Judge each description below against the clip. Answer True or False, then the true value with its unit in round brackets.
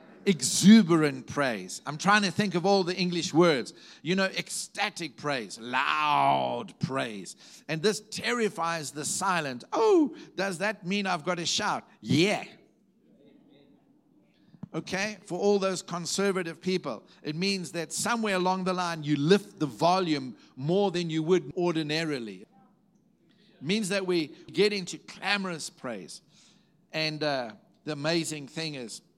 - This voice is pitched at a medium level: True (180 Hz)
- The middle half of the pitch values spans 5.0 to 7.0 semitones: False (3.8 semitones)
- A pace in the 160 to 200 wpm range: False (140 wpm)